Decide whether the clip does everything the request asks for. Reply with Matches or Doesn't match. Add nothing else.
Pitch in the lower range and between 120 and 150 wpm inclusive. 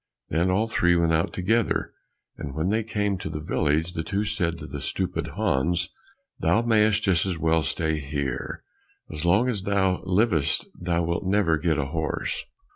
Doesn't match